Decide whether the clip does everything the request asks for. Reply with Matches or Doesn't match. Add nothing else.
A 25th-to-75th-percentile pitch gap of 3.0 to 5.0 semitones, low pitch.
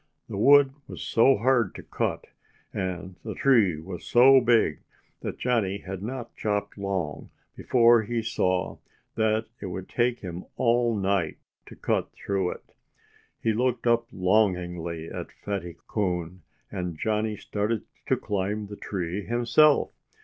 Matches